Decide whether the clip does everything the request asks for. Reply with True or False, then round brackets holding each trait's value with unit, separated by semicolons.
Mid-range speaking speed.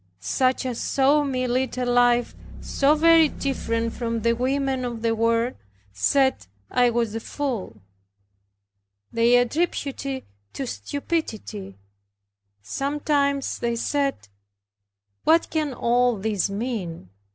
False (120 wpm)